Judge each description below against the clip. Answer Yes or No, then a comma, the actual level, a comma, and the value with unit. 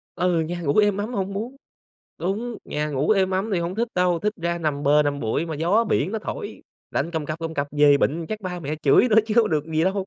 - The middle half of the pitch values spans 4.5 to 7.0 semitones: Yes, average, 5.1 semitones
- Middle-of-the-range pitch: Yes, medium, 175 Hz